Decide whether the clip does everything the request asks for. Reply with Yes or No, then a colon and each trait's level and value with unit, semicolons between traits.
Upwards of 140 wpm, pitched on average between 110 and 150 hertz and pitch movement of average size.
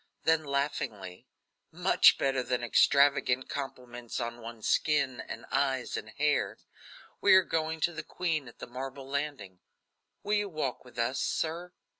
Yes: average, 150 wpm; low, 135 Hz; average, 4.0 semitones